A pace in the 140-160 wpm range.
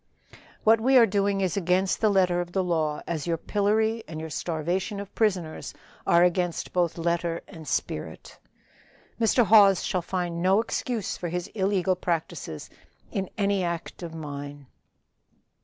Yes: average, 155 wpm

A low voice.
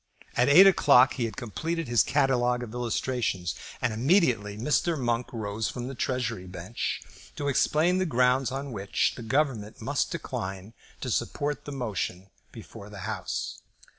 Yes: low, 125 Hz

